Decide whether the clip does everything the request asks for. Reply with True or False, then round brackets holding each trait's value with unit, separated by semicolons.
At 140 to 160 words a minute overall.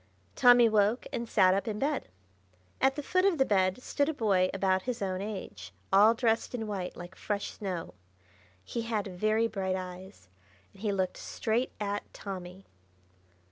False (170 wpm)